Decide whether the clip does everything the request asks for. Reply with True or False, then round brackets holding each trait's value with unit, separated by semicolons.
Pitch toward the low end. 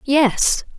False (265 Hz)